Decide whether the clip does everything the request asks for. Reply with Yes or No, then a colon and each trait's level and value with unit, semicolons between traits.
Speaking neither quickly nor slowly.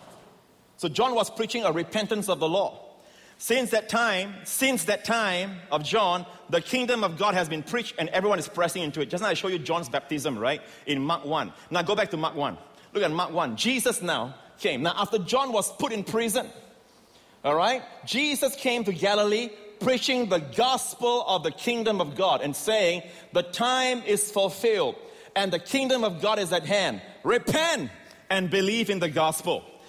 Yes: average, 190 wpm